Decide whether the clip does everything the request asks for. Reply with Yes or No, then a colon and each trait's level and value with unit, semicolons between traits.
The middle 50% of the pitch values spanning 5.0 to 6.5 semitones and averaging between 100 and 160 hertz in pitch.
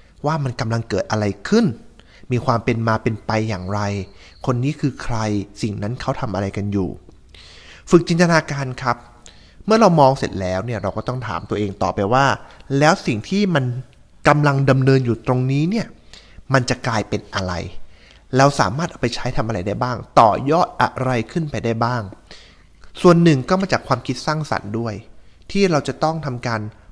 Yes: average, 5.3 semitones; low, 120 Hz